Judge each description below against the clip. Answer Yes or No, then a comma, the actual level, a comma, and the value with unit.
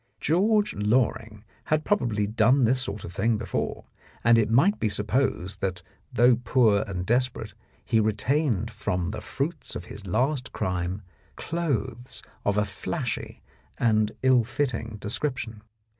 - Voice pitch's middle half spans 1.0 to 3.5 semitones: No, average, 4.0 semitones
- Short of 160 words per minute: Yes, average, 140 wpm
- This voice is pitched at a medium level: No, low, 115 Hz